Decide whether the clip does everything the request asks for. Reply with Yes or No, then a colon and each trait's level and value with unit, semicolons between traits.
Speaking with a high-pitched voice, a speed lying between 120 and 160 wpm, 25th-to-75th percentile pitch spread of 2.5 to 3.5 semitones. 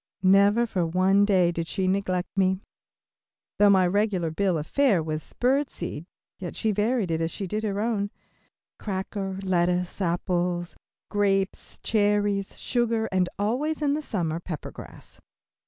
Yes: high, 195 Hz; average, 150 wpm; average, 2.9 semitones